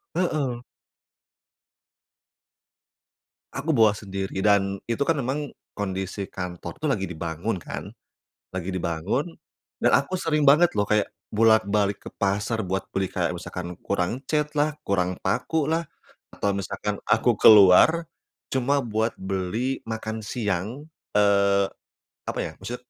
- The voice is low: Yes, low, 105 Hz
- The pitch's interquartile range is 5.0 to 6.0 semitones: Yes, wide, 5.5 semitones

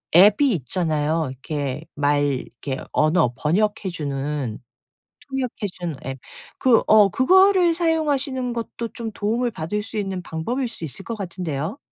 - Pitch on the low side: No, medium, 185 Hz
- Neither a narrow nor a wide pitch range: No, wide, 8.1 semitones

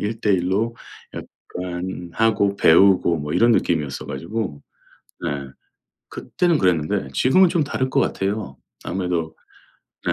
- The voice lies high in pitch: No, very low, 95 Hz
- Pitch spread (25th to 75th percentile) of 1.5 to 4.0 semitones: No, average, 5.1 semitones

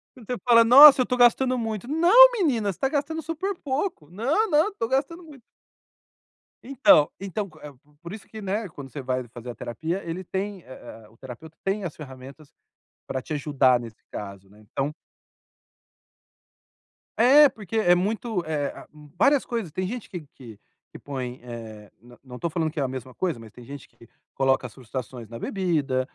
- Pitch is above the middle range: No, medium, 175 Hz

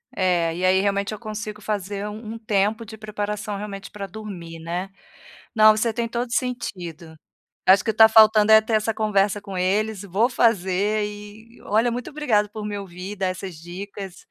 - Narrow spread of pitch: Yes, narrow, 2.2 semitones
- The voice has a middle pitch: No, high, 210 Hz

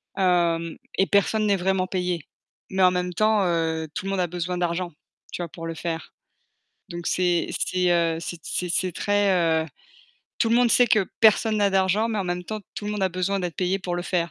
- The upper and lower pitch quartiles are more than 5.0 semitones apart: No, narrow, 2.4 semitones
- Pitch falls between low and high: Yes, medium, 180 Hz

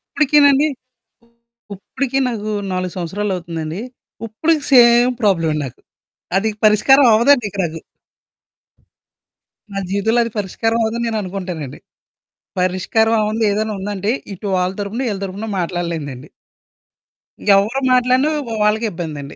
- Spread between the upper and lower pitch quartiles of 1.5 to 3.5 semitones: No, average, 4.4 semitones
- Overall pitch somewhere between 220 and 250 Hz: No, high, 210 Hz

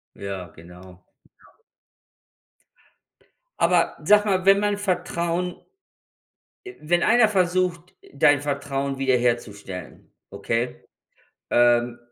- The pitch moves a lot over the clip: Yes, wide, 7.4 semitones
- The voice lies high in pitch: No, medium, 140 Hz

